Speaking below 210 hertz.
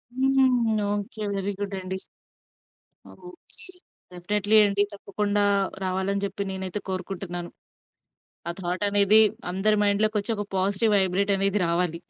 Yes: high, 200 Hz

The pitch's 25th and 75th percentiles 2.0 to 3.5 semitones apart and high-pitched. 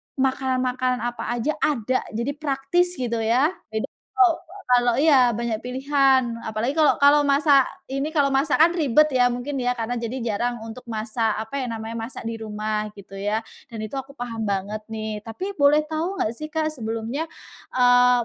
No: average, 3.9 semitones; very high, 250 Hz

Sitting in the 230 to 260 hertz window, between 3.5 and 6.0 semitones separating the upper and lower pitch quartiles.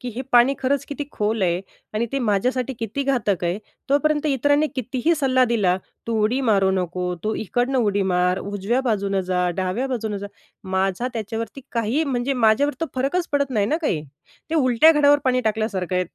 Yes: high, 235 Hz; average, 5.2 semitones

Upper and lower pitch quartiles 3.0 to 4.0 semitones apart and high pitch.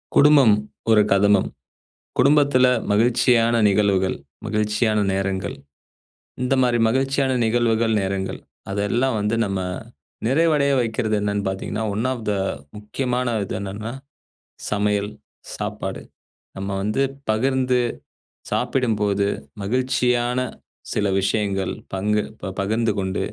No: average, 3.6 semitones; low, 110 Hz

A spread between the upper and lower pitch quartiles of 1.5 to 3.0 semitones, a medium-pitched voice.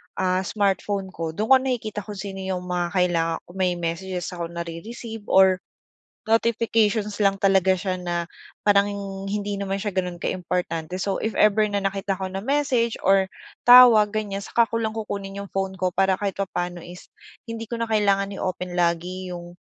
No: narrow, 2.6 semitones; high, 195 Hz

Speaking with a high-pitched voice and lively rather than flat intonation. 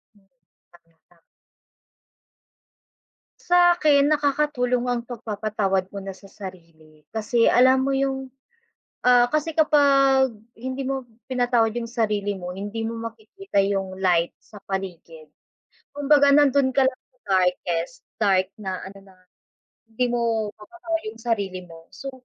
Yes: high, 230 Hz; wide, 5.7 semitones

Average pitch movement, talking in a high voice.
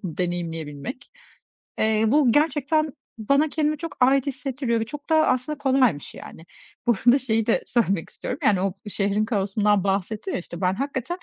No: wide, 6.0 semitones; high, 235 Hz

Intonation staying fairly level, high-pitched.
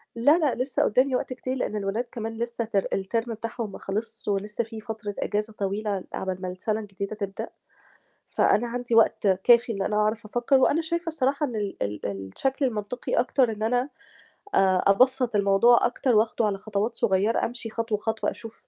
No: average, 3.2 semitones; high, 225 Hz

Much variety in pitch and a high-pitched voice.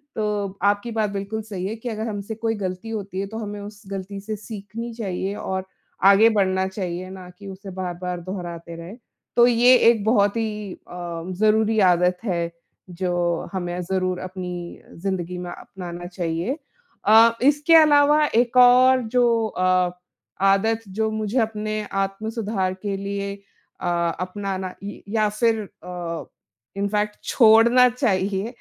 No: average, 3.2 semitones; high, 200 Hz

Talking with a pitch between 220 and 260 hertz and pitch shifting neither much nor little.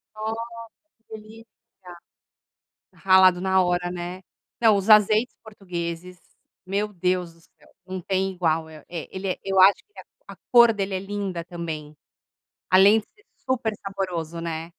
No: high, 190 Hz; average, 3.0 semitones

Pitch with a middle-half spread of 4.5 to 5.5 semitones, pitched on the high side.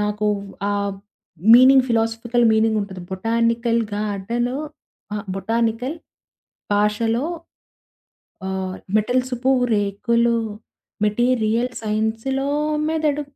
No: average, 2.8 semitones; high, 230 Hz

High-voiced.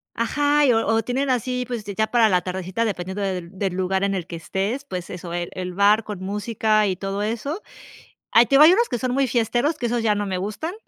Yes: high, 215 Hz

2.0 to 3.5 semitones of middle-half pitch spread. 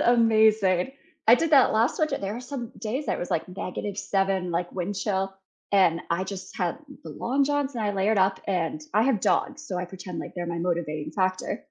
No: average, 4.4 semitones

